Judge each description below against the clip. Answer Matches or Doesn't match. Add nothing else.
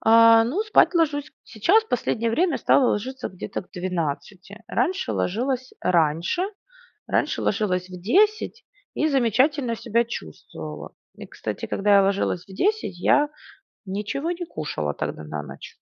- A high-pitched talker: Matches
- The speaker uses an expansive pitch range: Matches